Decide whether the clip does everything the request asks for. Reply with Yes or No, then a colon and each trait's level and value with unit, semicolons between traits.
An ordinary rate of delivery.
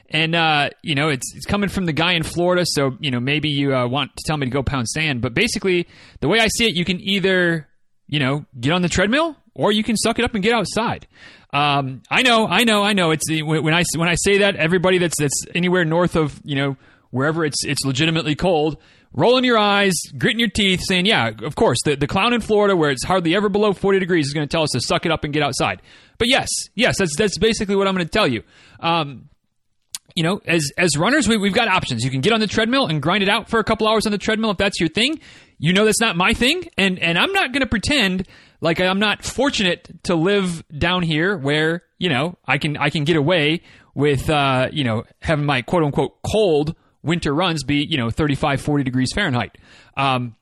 No: fast, 245 wpm